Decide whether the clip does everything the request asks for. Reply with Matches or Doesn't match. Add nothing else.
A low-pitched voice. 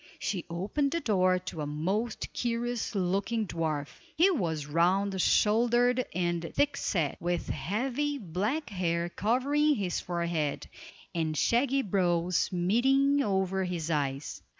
Doesn't match